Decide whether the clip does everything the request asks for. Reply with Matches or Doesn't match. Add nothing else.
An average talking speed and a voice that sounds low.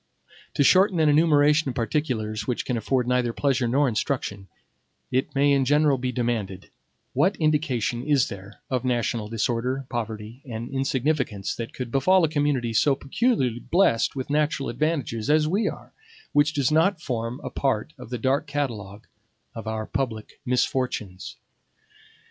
Matches